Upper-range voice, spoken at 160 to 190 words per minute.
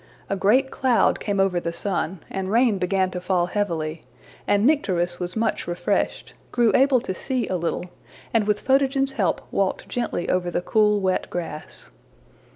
Yes: high, 195 Hz; average, 165 wpm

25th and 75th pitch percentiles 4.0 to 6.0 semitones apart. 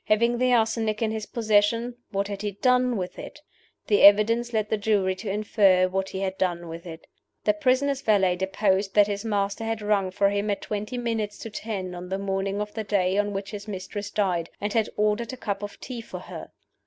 No: narrow, 2.4 semitones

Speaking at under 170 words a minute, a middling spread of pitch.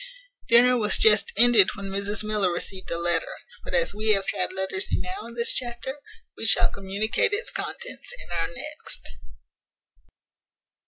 Yes: average, 155 wpm; average, 4.2 semitones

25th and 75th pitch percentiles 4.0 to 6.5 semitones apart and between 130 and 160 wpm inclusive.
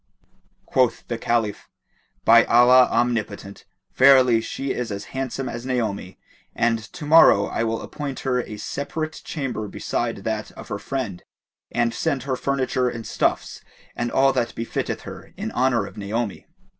No: average, 2.9 semitones; average, 155 wpm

